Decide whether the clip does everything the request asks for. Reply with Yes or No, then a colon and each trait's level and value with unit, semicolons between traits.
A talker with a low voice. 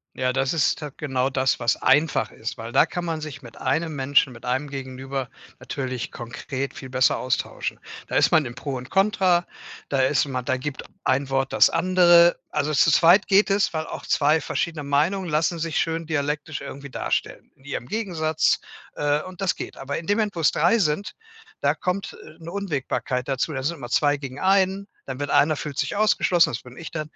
No: medium, 150 Hz